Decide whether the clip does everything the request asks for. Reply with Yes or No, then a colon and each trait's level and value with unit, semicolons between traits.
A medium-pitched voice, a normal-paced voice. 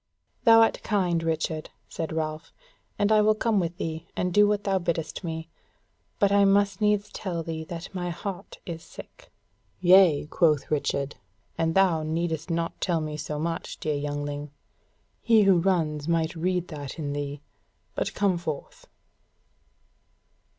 Yes: medium, 170 Hz; average, 155 wpm